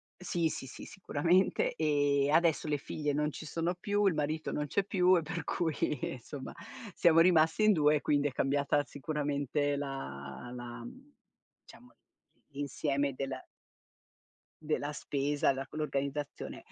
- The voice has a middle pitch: Yes, medium, 150 Hz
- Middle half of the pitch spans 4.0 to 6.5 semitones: No, average, 2.7 semitones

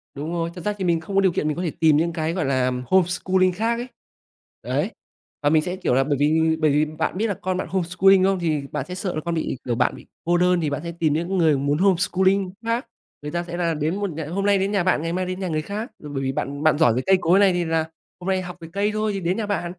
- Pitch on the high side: No, medium, 175 Hz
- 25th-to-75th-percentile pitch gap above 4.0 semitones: No, average, 3.4 semitones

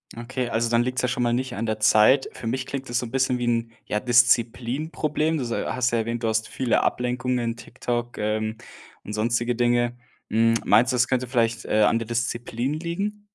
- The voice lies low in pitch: Yes, low, 120 Hz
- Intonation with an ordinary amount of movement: No, narrow, 1.7 semitones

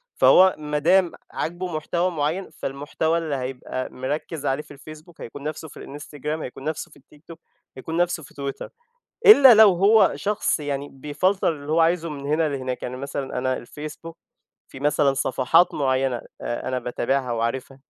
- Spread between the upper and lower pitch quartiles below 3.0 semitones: No, average, 3.6 semitones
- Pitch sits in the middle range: Yes, medium, 150 Hz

